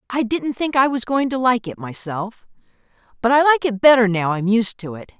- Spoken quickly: Yes, fast, 230 wpm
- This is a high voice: Yes, high, 230 Hz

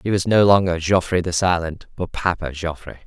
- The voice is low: Yes, very low, 90 Hz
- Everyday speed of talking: Yes, average, 195 wpm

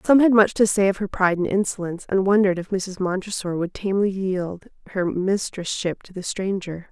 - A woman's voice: Yes, female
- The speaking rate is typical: No, fast, 210 wpm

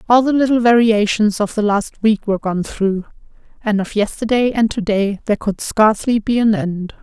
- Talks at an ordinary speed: Yes, average, 190 wpm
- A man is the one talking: No, female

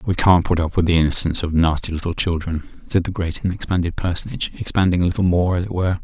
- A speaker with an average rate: No, fast, 240 wpm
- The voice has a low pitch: Yes, very low, 90 Hz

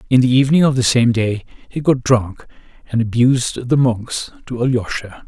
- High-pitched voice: No, low, 120 Hz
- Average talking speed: Yes, average, 180 wpm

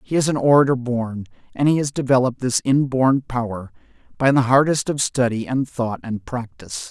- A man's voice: Yes, male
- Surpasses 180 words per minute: No, average, 175 wpm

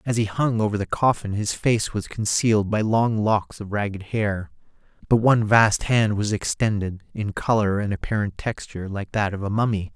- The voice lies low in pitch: Yes, low, 105 Hz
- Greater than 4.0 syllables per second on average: Yes, 5.0 syllables/s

